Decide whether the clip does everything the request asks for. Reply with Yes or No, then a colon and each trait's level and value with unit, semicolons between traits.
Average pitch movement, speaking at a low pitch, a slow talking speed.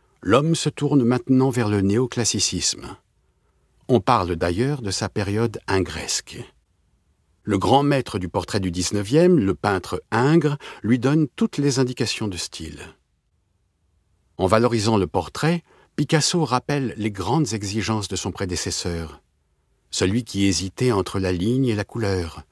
No: wide, 6.0 semitones; low, 105 Hz; slow, 140 wpm